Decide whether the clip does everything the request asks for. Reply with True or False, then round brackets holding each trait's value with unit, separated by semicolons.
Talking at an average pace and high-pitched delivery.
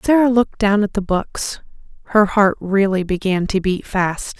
True (175 wpm; 200 Hz)